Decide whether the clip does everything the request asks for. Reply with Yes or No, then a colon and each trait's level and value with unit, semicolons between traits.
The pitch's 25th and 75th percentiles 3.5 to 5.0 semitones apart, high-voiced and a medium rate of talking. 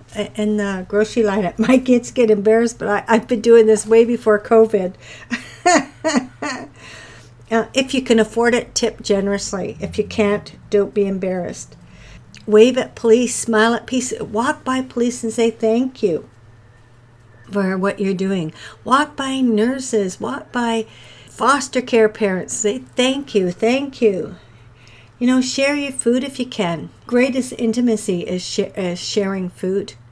Yes: average, 3.8 semitones; high, 220 Hz; average, 150 wpm